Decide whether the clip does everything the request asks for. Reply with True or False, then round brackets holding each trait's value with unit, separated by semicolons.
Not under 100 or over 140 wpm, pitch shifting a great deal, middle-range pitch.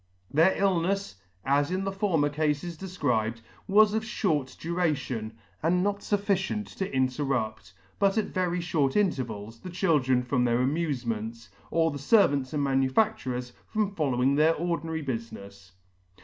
True (135 wpm; 6.6 semitones; 150 Hz)